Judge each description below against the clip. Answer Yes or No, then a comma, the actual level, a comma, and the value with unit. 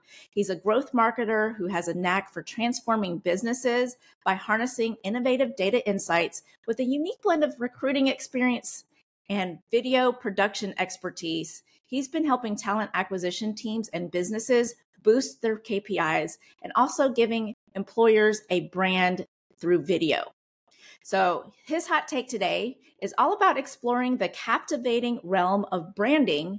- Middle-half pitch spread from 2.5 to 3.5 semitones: No, average, 4.8 semitones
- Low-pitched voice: No, high, 220 Hz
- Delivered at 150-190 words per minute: No, slow, 135 wpm